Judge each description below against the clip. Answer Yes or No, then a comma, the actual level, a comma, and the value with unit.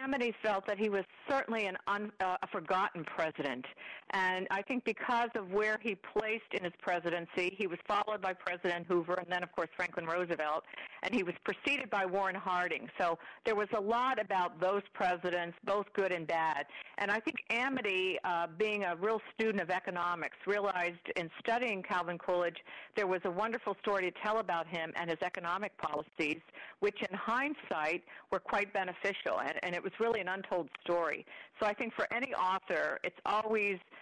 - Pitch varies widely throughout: No, average, 3.3 semitones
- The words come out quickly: No, average, 185 wpm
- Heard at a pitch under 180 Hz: No, high, 195 Hz